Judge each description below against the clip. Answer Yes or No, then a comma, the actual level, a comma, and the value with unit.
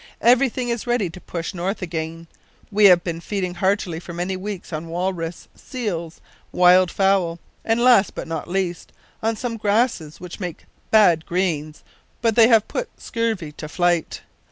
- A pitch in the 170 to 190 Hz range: Yes, medium, 185 Hz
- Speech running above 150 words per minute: Yes, average, 160 wpm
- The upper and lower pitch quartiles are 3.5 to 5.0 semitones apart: Yes, average, 4.4 semitones